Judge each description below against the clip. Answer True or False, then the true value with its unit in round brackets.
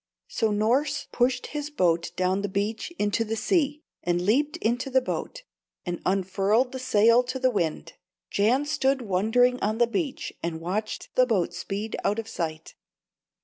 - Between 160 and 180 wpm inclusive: True (165 wpm)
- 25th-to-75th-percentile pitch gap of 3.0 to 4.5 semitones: False (4.9 semitones)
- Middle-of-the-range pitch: False (225 Hz)